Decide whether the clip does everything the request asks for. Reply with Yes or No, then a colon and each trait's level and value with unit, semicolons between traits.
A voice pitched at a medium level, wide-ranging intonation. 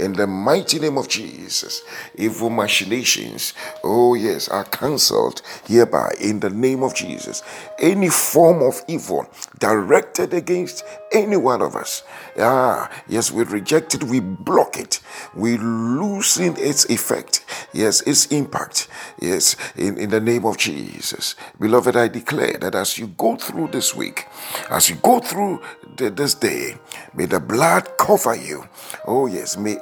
No: low, 125 Hz; wide, 6.1 semitones